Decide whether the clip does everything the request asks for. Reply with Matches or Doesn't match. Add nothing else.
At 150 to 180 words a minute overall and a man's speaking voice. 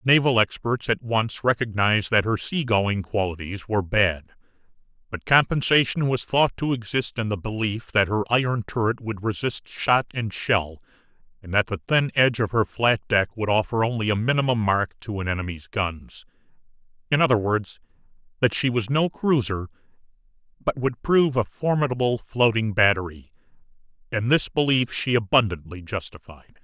Matches